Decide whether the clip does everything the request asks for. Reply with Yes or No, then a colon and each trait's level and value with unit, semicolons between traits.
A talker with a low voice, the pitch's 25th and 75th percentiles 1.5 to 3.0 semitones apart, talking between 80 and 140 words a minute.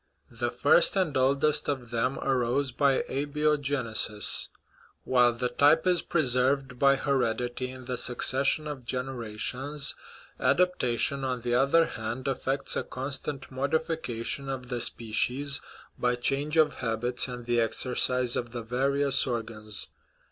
Yes: low, 130 Hz; narrow, 2.5 semitones; slow, 135 wpm